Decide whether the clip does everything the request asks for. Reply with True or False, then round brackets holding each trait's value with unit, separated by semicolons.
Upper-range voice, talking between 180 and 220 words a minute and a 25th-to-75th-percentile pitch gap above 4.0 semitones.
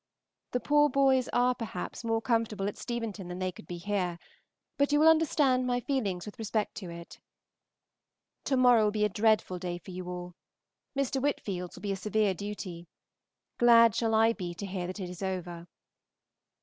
True (210 Hz; 185 wpm; 5.1 semitones)